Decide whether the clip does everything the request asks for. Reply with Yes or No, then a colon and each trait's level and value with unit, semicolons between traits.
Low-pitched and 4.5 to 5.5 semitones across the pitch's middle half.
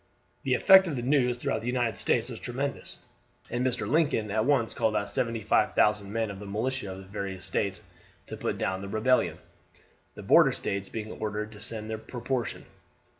No: low, 110 Hz; average, 3.3 semitones